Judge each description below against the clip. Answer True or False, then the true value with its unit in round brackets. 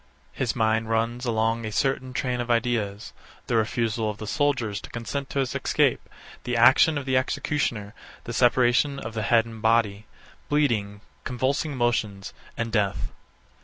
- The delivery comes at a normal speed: True (160 wpm)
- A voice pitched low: True (115 Hz)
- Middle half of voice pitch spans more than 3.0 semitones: False (2.7 semitones)